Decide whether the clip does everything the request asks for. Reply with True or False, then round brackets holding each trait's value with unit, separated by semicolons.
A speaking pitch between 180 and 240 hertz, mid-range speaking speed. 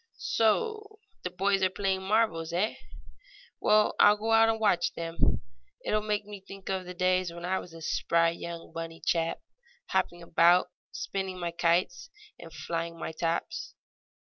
True (185 Hz; 165 wpm)